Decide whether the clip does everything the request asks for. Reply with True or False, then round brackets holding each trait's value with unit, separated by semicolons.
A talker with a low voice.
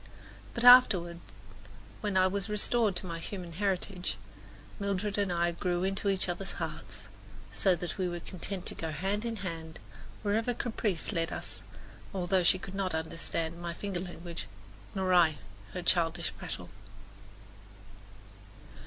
False (185 Hz)